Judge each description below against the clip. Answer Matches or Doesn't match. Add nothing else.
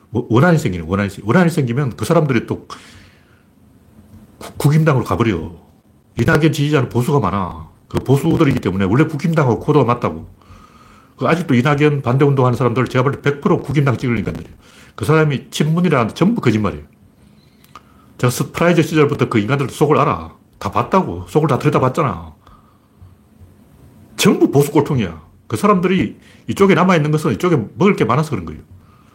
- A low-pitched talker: Matches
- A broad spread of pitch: Matches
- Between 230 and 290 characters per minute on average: Doesn't match